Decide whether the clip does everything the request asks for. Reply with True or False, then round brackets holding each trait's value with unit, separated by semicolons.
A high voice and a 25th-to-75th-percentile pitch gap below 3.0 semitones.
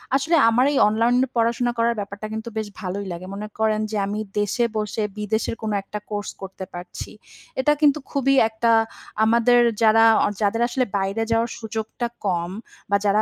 True (220 Hz; 2.5 semitones)